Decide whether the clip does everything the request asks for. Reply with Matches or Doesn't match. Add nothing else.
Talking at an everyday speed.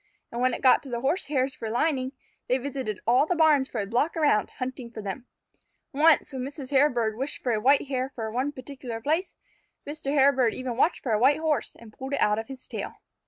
Doesn't match